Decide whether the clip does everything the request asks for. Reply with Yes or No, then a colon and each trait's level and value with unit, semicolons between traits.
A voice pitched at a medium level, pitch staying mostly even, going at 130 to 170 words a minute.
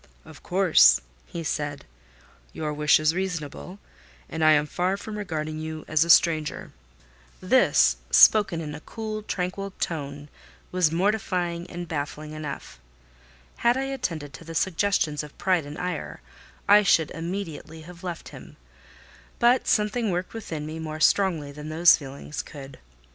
No: medium, 165 Hz; average, 3.7 semitones; average, 150 wpm